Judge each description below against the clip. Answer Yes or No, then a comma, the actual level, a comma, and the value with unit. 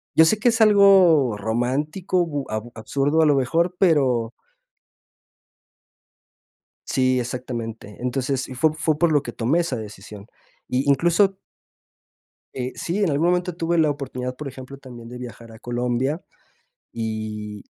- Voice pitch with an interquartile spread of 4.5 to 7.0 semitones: Yes, average, 5.3 semitones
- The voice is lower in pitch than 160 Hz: Yes, low, 135 Hz